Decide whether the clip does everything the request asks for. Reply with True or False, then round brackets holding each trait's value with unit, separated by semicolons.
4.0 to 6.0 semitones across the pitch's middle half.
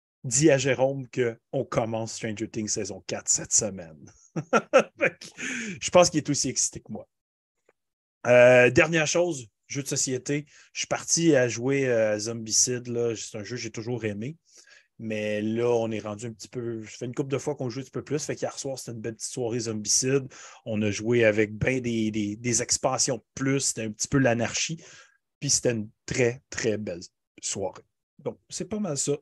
False (3.6 semitones)